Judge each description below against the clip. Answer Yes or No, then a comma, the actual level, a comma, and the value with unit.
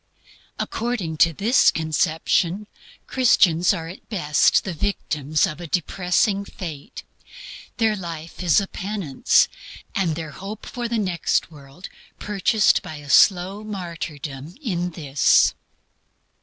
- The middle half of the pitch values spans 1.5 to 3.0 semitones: No, average, 4.3 semitones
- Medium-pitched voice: Yes, medium, 175 Hz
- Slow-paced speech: Yes, slow, 120 wpm